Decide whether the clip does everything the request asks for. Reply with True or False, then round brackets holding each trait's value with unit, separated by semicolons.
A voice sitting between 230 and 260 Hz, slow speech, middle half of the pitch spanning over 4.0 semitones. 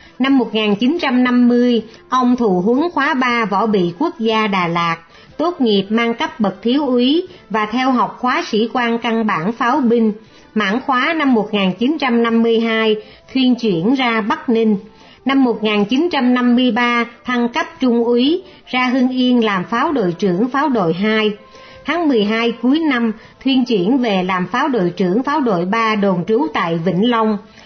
False (235 Hz; 160 wpm; 2.9 semitones)